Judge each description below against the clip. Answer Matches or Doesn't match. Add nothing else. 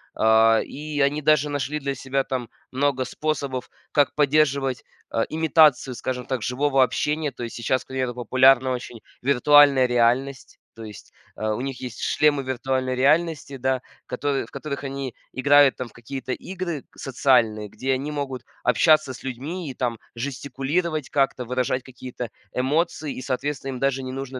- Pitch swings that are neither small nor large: Doesn't match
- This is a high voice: Doesn't match